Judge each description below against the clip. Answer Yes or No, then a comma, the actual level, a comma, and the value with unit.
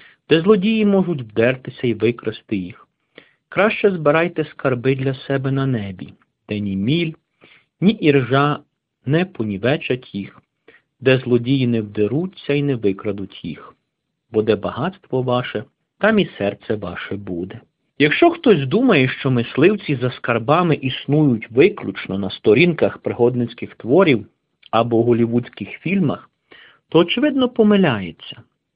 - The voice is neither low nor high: No, low, 130 Hz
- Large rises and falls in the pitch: Yes, wide, 6.4 semitones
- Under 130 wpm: Yes, average, 120 wpm